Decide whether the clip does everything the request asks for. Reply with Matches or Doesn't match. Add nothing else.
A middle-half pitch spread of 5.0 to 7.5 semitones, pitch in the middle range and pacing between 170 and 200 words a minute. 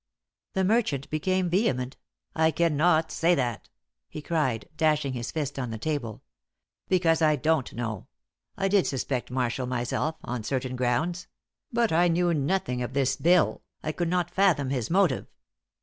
Doesn't match